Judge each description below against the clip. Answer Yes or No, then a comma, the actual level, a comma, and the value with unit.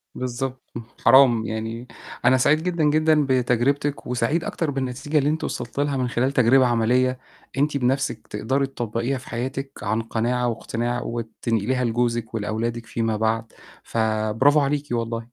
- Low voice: Yes, low, 125 Hz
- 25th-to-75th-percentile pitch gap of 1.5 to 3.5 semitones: Yes, average, 3.0 semitones